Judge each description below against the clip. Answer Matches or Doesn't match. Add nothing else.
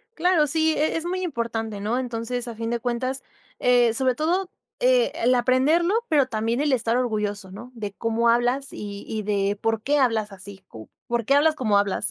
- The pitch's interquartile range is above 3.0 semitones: Matches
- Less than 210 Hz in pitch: Doesn't match